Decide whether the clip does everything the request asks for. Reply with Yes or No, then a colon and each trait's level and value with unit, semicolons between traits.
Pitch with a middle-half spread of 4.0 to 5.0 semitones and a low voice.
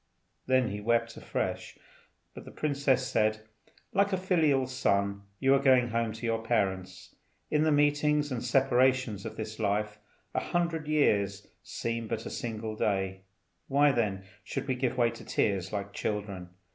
Yes: average, 4.7 semitones; low, 115 Hz